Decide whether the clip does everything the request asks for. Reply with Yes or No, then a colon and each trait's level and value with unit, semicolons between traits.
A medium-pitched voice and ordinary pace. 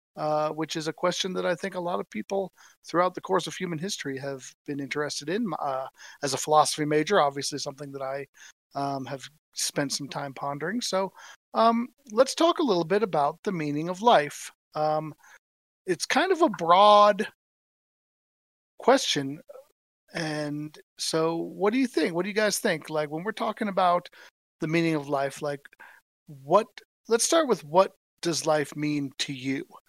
Yes: medium, 165 Hz; average, 175 wpm